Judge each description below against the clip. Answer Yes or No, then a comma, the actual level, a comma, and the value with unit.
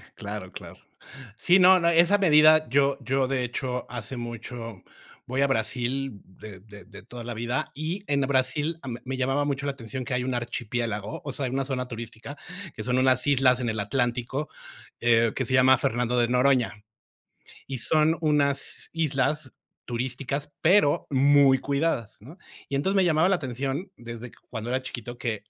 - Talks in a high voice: No, low, 130 Hz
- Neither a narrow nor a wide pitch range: Yes, average, 3.0 semitones